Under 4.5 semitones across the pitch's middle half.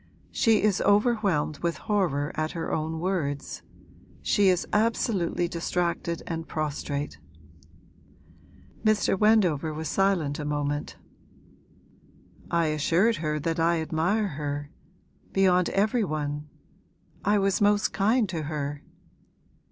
No: average, 4.8 semitones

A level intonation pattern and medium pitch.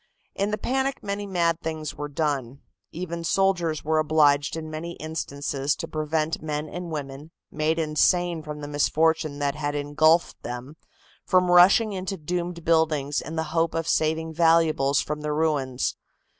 Yes: narrow, 2.3 semitones; medium, 155 Hz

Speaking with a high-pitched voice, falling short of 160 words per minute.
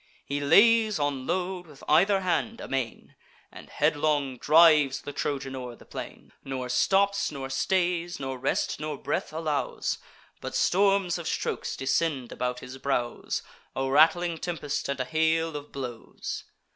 No: medium, 150 Hz; average, 145 wpm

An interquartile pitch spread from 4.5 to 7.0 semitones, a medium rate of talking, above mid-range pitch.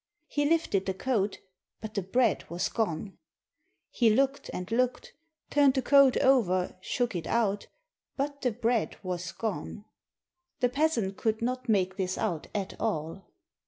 Yes: average, 5.1 semitones; average, 155 wpm; high, 220 Hz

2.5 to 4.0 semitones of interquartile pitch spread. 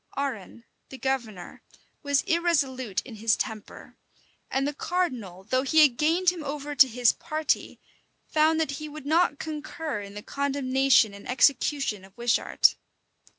No: average, 4.6 semitones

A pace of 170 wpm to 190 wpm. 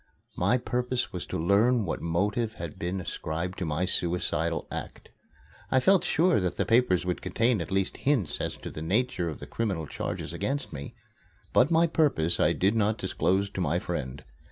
Yes: average, 185 wpm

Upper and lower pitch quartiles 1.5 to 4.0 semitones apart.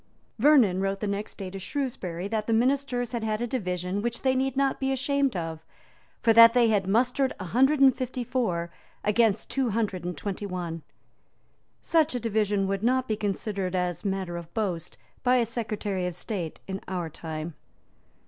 No: average, 5.1 semitones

